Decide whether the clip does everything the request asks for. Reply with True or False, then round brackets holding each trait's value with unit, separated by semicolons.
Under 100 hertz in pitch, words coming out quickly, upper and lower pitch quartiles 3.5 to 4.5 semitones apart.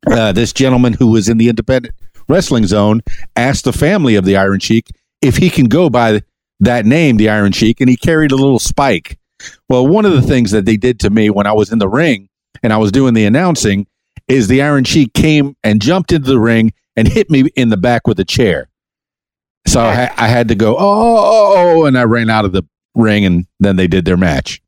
False (115 Hz; 230 wpm; 4.1 semitones)